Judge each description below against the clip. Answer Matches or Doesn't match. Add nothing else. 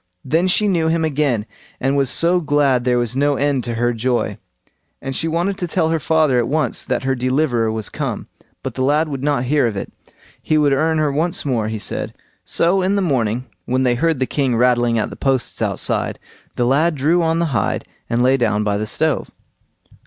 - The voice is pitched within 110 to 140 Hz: Matches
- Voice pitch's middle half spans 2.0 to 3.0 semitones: Doesn't match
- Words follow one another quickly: Matches